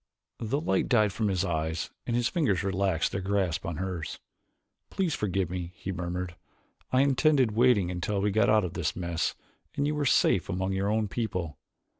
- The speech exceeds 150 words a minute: Yes, average, 185 wpm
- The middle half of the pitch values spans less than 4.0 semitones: No, average, 4.5 semitones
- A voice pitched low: Yes, low, 100 Hz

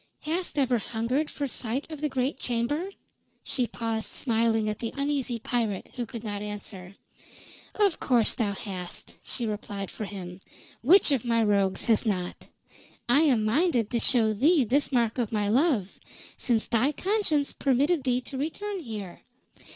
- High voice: Yes, high, 235 Hz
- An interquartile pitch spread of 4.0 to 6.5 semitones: Yes, average, 4.8 semitones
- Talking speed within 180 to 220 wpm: No, average, 160 wpm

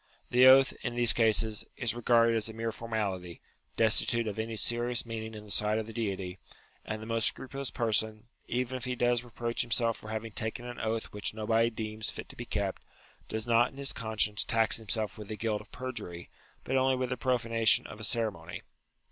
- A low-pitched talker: Yes, low, 115 Hz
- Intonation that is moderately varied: No, narrow, 1.8 semitones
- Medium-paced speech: No, fast, 210 wpm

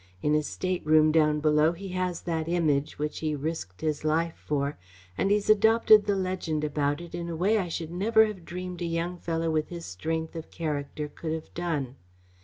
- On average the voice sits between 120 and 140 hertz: No, medium, 165 Hz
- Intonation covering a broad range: No, average, 2.9 semitones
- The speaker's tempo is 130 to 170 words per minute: No, average, 200 wpm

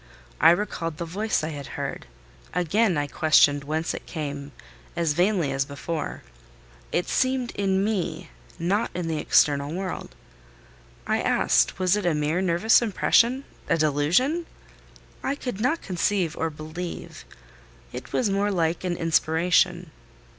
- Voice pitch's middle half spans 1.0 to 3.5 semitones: No, average, 4.3 semitones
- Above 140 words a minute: No, slow, 135 wpm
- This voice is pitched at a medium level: Yes, medium, 175 Hz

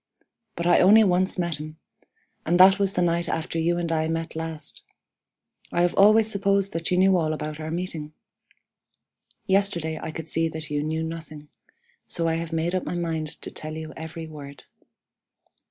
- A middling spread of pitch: No, narrow, 2.3 semitones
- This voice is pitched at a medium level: Yes, medium, 165 Hz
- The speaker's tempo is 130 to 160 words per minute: No, average, 185 wpm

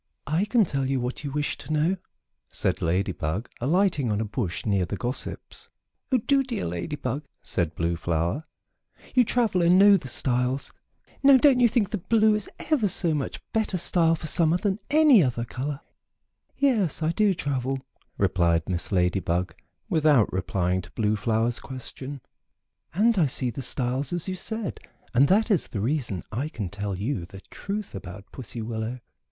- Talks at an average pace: Yes, average, 175 wpm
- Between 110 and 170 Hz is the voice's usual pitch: Yes, low, 135 Hz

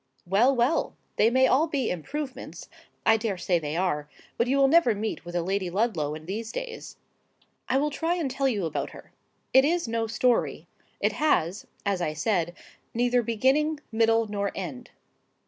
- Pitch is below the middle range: No, high, 225 Hz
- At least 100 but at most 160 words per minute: No, average, 175 wpm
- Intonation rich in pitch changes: Yes, wide, 6.4 semitones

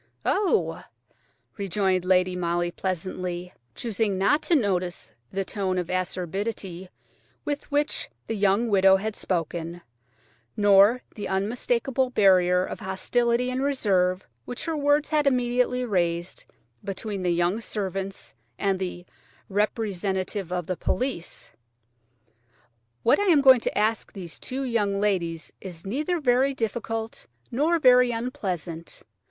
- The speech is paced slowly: Yes, slow, 120 wpm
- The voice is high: Yes, high, 195 Hz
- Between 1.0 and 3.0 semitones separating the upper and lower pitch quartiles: No, average, 5.1 semitones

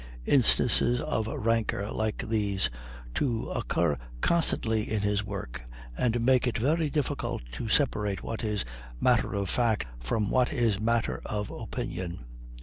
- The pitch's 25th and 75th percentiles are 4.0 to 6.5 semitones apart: No, average, 3.2 semitones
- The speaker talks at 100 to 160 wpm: Yes, average, 140 wpm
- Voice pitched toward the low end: Yes, low, 110 Hz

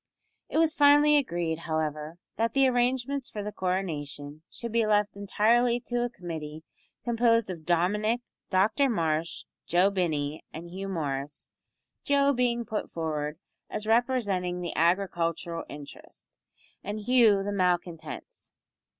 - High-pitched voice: Yes, high, 195 Hz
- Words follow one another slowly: Yes, slow, 130 wpm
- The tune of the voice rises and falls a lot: Yes, wide, 6.2 semitones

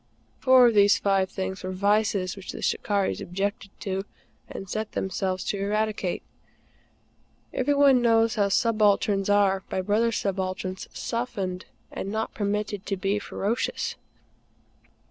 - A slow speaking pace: Yes, slow, 130 wpm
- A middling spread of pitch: No, narrow, 2.1 semitones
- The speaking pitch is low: No, high, 200 Hz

